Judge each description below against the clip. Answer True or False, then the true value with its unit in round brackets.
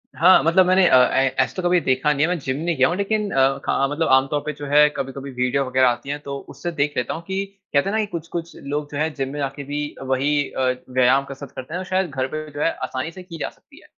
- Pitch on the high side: False (145 Hz)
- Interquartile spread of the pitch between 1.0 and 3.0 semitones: False (4.0 semitones)